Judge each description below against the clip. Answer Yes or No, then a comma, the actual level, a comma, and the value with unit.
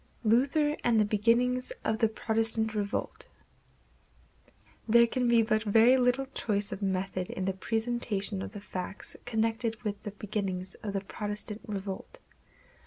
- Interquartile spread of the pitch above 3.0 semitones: No, average, 2.7 semitones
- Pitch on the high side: Yes, high, 220 Hz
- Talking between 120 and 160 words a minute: Yes, average, 145 wpm